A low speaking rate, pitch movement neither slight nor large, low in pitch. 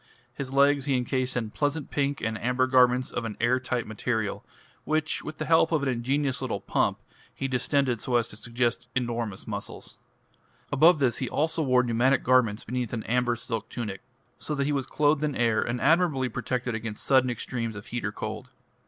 No: average, 195 wpm; average, 3.0 semitones; low, 125 Hz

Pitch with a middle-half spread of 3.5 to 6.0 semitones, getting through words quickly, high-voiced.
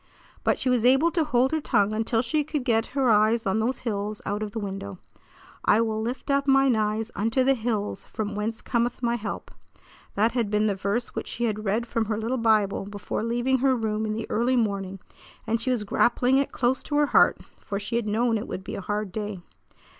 No: average, 2.9 semitones; fast, 225 wpm; high, 225 Hz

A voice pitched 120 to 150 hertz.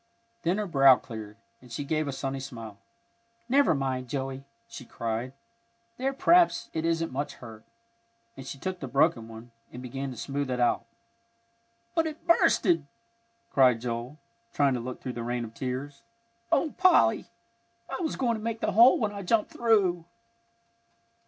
Yes: low, 135 Hz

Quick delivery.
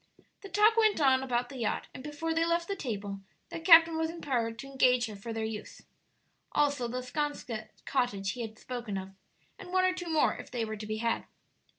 Yes: fast, 215 wpm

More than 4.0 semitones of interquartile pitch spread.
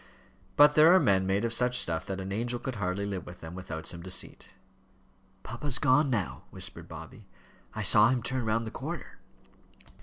Yes: average, 5.1 semitones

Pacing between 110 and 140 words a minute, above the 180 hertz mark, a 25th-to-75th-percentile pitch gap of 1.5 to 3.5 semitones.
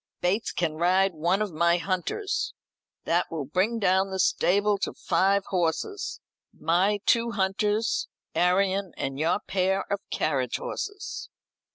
Yes: slow, 135 wpm; high, 190 Hz; average, 2.8 semitones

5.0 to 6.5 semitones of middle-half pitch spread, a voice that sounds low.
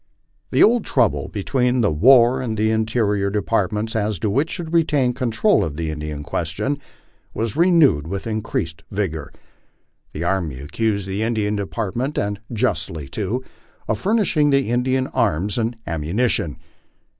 Yes: average, 5.3 semitones; low, 110 Hz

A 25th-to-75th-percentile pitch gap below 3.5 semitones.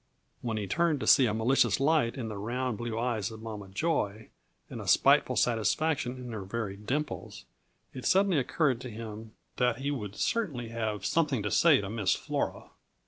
No: average, 4.2 semitones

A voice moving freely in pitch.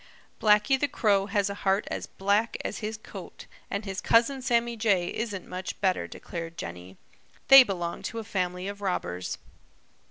No: average, 3.6 semitones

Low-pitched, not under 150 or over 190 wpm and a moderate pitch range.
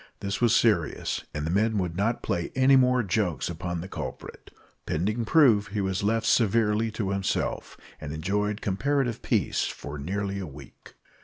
Yes: low, 100 Hz; average, 165 wpm; average, 4.1 semitones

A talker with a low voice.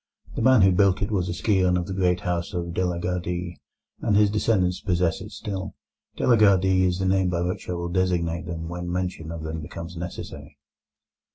Yes: very low, 90 Hz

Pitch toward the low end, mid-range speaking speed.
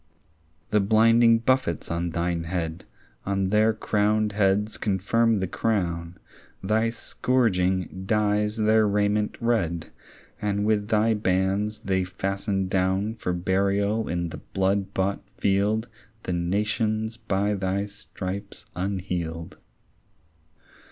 No: low, 100 Hz; slow, 110 wpm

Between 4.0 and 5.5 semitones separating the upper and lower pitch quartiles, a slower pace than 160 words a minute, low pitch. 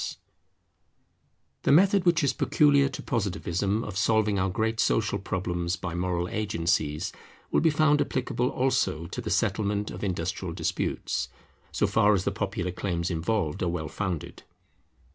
Yes: average, 4.6 semitones; average, 150 wpm; low, 100 Hz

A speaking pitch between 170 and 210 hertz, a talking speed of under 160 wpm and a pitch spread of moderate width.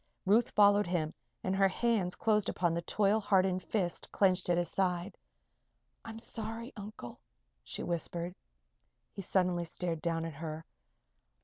Yes: medium, 185 Hz; average, 140 wpm; average, 3.3 semitones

